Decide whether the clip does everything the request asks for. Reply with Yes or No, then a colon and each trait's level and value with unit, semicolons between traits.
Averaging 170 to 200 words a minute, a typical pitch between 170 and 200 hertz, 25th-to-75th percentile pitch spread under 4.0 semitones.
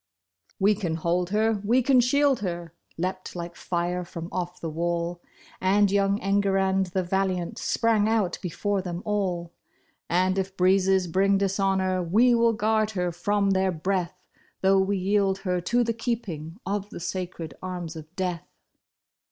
No: average, 160 wpm; high, 190 Hz; narrow, 2.6 semitones